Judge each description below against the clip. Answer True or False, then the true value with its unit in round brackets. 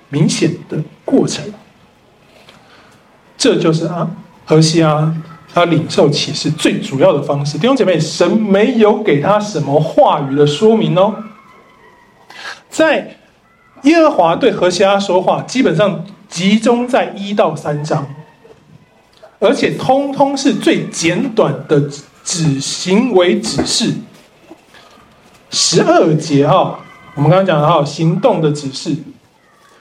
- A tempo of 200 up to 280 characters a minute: False (185 characters per minute)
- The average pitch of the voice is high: False (175 Hz)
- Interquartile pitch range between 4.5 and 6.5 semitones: True (5.2 semitones)